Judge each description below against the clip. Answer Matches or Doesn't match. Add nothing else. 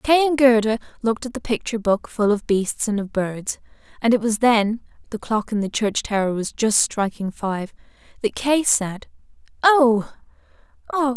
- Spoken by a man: Doesn't match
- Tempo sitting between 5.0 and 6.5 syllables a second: Doesn't match